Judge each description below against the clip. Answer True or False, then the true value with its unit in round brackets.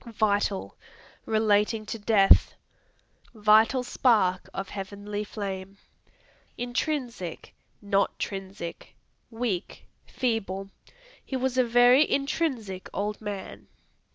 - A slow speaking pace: True (90 wpm)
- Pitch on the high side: True (210 Hz)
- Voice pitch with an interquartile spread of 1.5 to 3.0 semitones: False (3.6 semitones)